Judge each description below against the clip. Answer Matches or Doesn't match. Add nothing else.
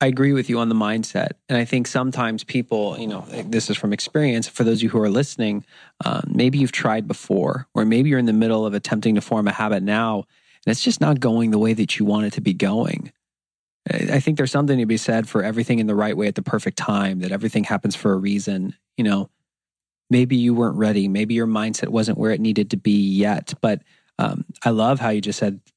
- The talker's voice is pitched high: Doesn't match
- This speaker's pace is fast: Matches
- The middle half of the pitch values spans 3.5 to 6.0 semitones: Doesn't match